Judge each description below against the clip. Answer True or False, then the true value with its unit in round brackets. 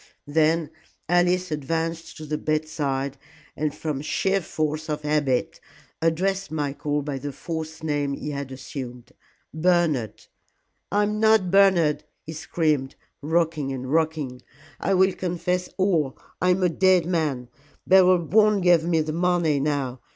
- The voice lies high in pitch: False (160 Hz)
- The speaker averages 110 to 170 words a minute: True (145 wpm)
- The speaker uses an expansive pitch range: False (3.5 semitones)